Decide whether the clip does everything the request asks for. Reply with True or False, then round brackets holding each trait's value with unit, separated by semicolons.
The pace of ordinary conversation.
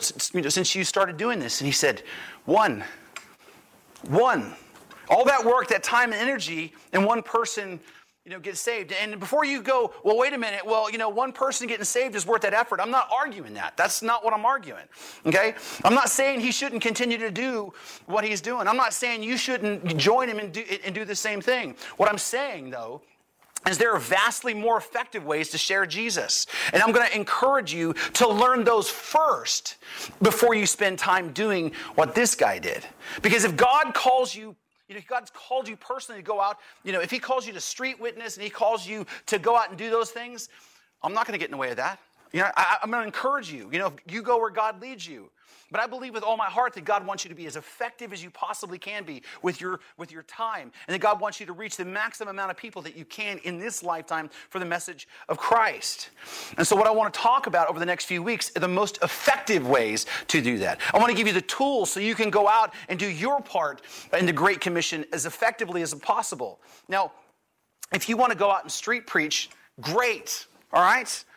False (235 wpm)